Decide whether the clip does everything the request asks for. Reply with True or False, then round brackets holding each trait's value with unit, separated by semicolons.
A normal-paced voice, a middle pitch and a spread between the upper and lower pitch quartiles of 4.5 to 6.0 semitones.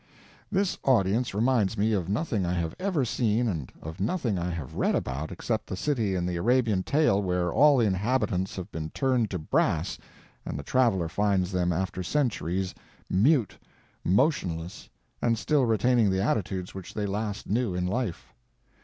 False (170 wpm; 100 Hz; 5.2 semitones)